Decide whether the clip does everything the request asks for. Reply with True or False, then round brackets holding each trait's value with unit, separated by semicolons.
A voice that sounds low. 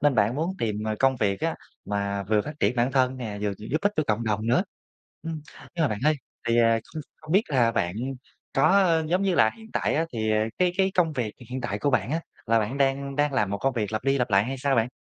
True (125 Hz)